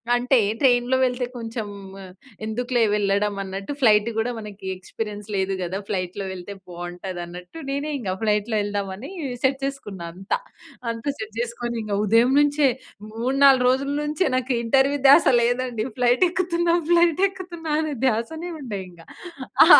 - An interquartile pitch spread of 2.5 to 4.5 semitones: No, average, 5.1 semitones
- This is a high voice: Yes, high, 235 Hz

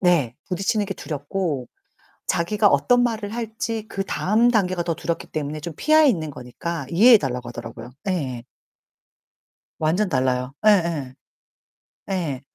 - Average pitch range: No, wide, 7.1 semitones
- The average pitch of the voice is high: No, medium, 170 Hz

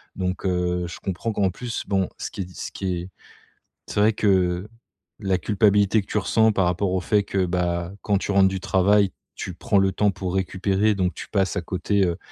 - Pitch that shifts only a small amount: Yes, narrow, 2.0 semitones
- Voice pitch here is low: Yes, very low, 95 Hz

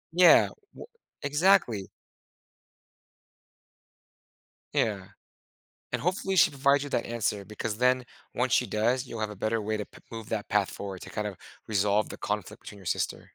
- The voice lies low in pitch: Yes, low, 110 Hz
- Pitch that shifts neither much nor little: Yes, average, 3.8 semitones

